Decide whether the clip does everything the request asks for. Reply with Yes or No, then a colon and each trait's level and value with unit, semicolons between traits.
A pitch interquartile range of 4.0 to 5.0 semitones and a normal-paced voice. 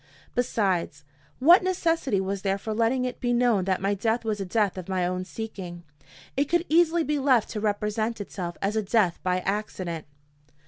Yes: average, 4.5 semitones; average, 185 wpm